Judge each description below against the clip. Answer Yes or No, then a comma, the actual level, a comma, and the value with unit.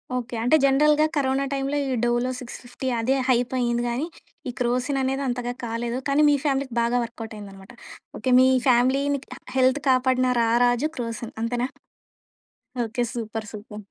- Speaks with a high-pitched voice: Yes, high, 245 Hz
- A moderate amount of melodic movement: No, narrow, 2.2 semitones